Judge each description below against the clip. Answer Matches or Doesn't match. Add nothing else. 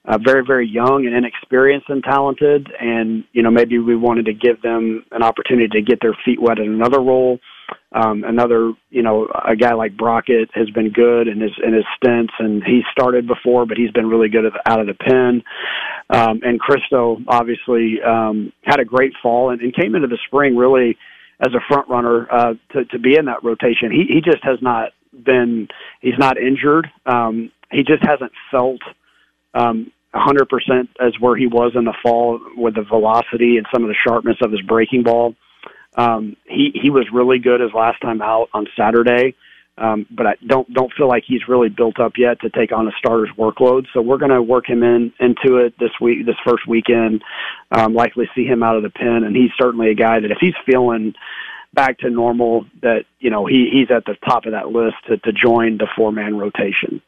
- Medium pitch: Doesn't match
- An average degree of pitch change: Doesn't match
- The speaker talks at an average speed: Doesn't match